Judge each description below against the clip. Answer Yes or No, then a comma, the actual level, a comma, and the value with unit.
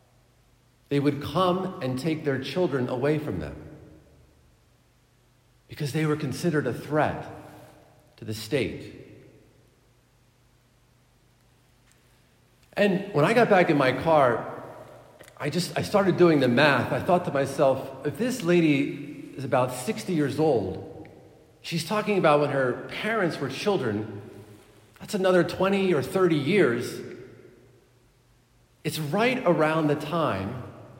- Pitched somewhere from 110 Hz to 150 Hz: Yes, medium, 140 Hz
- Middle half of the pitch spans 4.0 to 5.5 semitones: Yes, average, 4.9 semitones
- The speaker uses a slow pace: Yes, slow, 125 wpm